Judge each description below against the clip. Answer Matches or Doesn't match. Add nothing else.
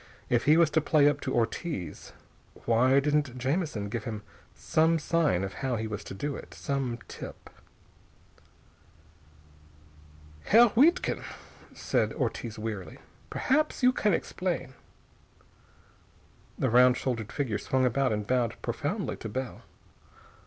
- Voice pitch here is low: Matches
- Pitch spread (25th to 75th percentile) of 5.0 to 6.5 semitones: Matches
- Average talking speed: Doesn't match